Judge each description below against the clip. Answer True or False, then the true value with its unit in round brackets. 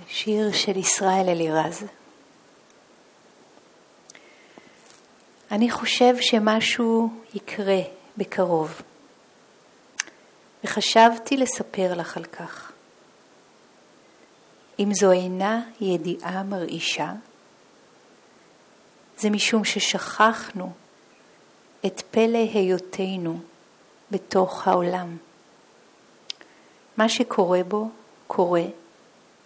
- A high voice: True (200 Hz)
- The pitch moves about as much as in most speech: True (3.4 semitones)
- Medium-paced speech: False (65 wpm)